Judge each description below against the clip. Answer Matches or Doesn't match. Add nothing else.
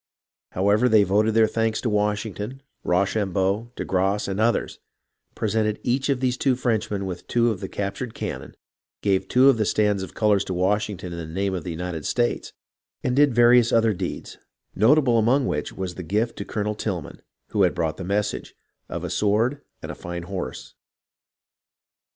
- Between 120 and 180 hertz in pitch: Doesn't match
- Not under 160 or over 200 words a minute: Matches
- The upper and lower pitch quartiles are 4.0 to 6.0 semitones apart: Doesn't match